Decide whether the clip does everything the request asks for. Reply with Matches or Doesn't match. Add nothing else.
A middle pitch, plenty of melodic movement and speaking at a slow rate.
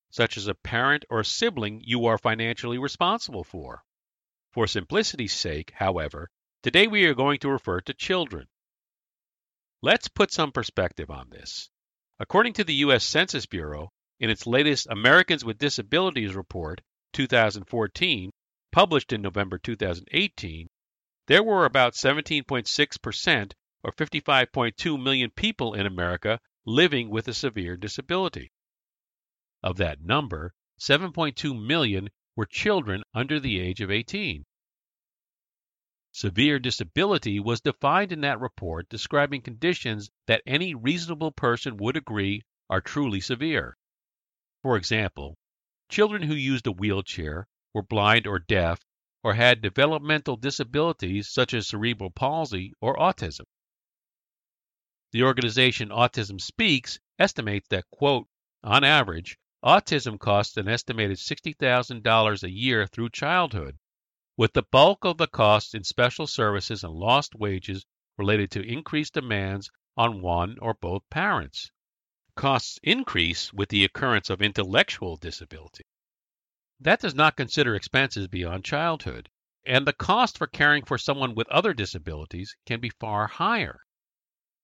Doesn't match